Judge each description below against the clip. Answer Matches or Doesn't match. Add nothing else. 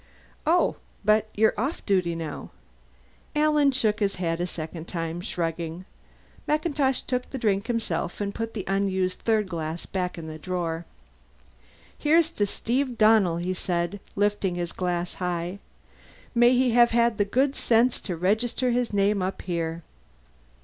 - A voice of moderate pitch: Doesn't match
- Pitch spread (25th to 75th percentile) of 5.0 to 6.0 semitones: Matches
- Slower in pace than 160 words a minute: Matches